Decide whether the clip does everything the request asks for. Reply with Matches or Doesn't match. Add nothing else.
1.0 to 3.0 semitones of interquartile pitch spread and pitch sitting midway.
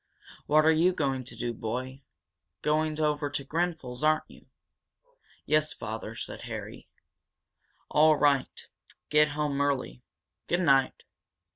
Matches